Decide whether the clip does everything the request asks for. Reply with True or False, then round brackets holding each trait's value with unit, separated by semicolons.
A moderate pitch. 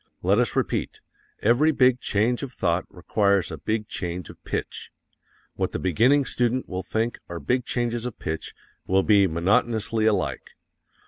False (110 Hz)